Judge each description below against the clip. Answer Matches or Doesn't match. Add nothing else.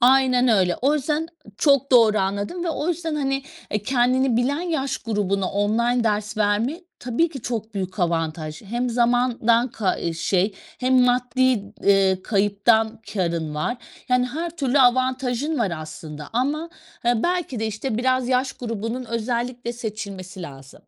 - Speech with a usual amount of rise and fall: Matches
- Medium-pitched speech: Doesn't match